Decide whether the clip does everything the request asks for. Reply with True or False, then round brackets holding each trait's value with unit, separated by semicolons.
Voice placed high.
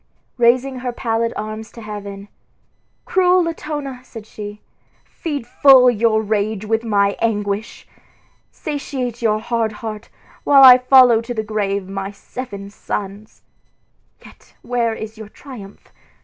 True (225 Hz)